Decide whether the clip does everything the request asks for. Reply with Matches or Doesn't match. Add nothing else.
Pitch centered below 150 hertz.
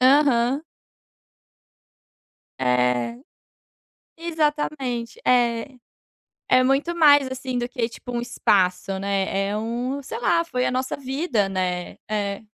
Doesn't match